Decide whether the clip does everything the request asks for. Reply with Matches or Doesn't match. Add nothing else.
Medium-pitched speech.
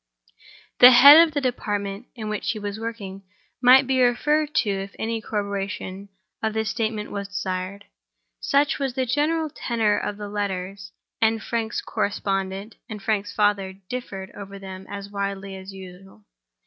Doesn't match